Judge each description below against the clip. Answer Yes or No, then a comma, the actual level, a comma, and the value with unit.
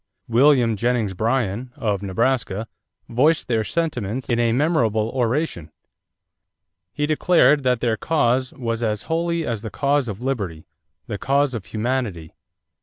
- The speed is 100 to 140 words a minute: Yes, slow, 135 wpm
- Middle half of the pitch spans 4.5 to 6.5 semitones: No, average, 4.1 semitones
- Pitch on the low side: Yes, low, 120 Hz